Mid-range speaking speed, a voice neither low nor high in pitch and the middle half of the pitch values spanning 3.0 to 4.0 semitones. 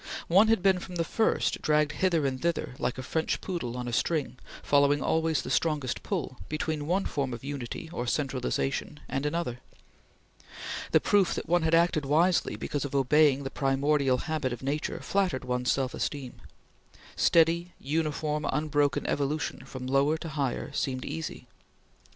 Yes: average, 165 wpm; medium, 145 Hz; average, 3.5 semitones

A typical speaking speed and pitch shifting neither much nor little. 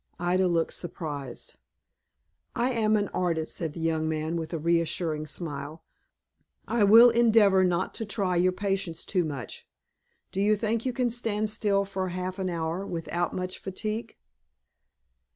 Yes: average, 150 wpm; average, 4.2 semitones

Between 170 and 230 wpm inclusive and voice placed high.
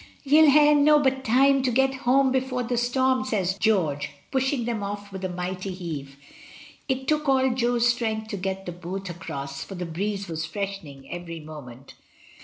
Yes: average, 175 wpm; high, 210 Hz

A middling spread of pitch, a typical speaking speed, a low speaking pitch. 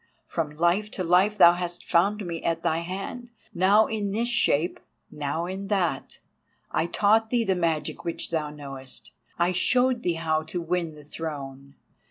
No: average, 3.9 semitones; average, 170 wpm; medium, 175 Hz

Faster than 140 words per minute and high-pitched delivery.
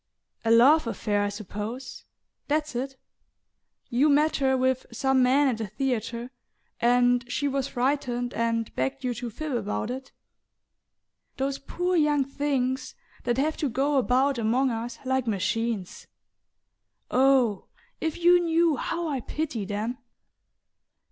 No: slow, 135 wpm; very high, 255 Hz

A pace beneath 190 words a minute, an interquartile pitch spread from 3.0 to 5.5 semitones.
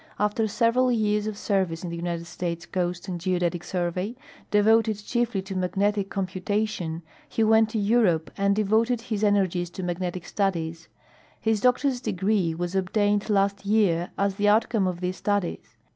Yes: average, 160 wpm; average, 3.3 semitones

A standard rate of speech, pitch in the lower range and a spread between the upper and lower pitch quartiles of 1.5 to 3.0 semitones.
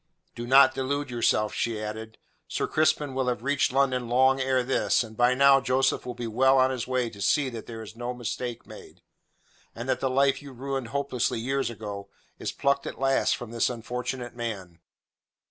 Yes: average, 195 wpm; low, 125 Hz; narrow, 2.4 semitones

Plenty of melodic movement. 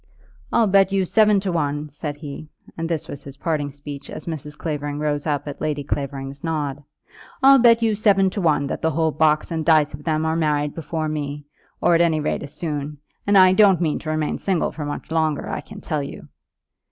No: average, 2.7 semitones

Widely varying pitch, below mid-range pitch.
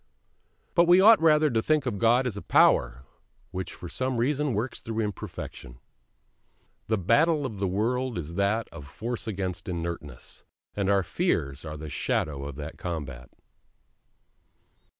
Yes: wide, 7.6 semitones; low, 100 Hz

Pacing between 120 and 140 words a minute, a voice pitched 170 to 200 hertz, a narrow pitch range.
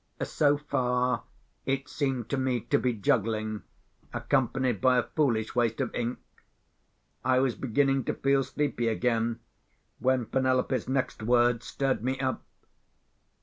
No: slow, 135 wpm; low, 125 Hz; narrow, 2.3 semitones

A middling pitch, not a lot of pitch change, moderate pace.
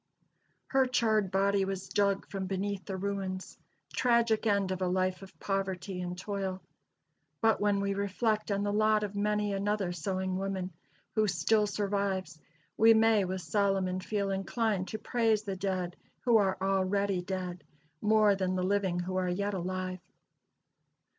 No: high, 195 Hz; narrow, 1.9 semitones; average, 155 wpm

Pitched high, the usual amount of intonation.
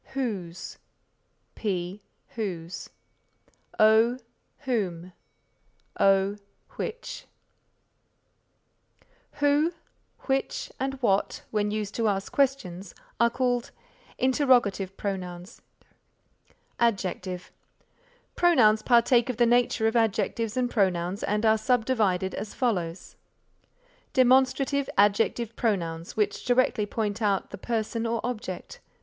Yes: high, 220 Hz; average, 4.1 semitones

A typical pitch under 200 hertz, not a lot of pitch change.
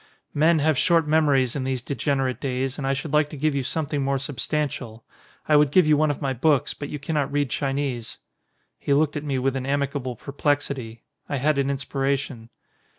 Yes: medium, 140 Hz; narrow, 1.9 semitones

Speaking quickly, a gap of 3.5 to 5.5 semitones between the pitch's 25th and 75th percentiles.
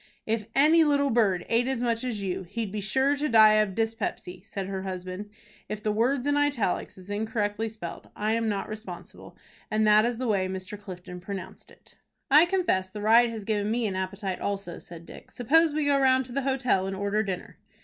Yes: fast, 210 wpm; average, 4.0 semitones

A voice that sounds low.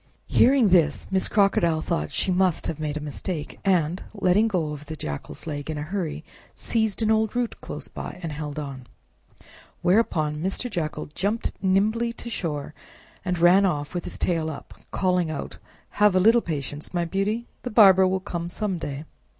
No: medium, 180 Hz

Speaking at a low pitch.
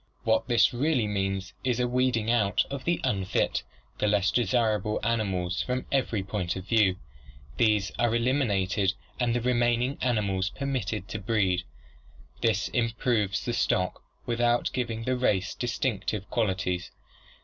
Yes: low, 110 Hz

